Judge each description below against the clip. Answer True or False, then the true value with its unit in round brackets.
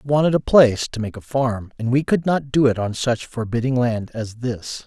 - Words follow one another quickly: True (245 wpm)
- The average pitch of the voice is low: True (125 Hz)